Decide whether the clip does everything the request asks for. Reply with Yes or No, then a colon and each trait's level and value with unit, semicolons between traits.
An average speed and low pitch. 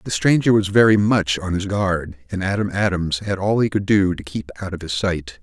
No: fast, 245 wpm; very low, 95 Hz